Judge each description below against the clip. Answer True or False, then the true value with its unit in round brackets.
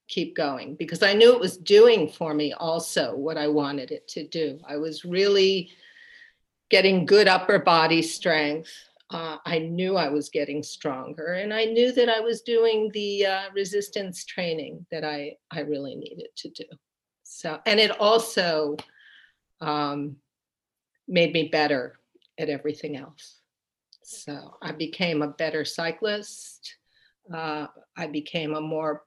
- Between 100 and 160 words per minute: True (150 wpm)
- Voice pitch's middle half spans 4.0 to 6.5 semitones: True (5.3 semitones)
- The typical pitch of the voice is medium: True (165 Hz)